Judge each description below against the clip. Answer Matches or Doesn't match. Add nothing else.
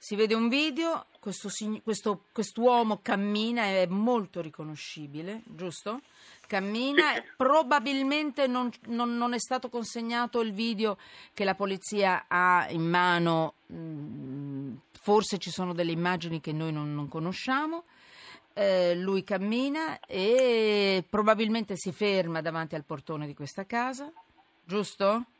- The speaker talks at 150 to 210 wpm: Doesn't match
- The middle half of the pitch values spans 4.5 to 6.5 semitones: Matches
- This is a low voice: Doesn't match